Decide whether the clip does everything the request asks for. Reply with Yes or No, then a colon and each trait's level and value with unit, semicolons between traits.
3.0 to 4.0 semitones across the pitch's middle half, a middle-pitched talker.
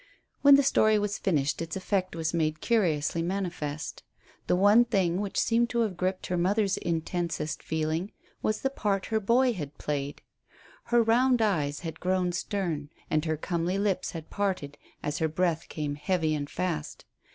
No: average, 4.5 semitones; medium, 180 Hz